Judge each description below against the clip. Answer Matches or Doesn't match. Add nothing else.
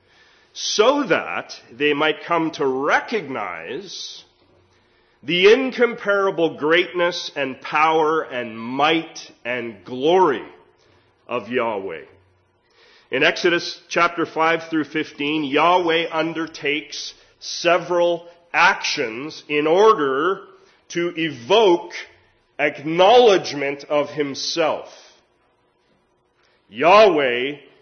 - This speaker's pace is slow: Matches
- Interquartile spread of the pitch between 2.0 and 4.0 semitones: Matches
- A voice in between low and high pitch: Matches